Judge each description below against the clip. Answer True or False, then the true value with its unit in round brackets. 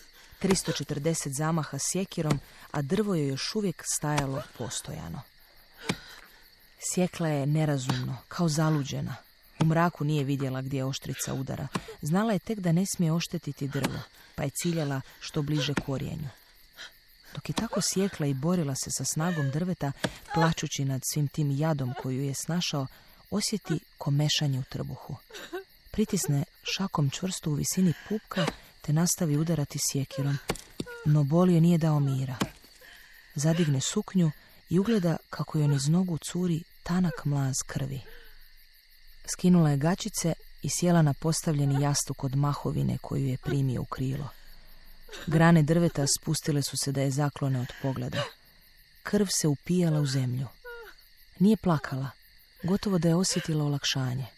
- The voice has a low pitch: False (155 Hz)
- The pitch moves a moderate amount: True (3.7 semitones)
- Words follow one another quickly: False (135 wpm)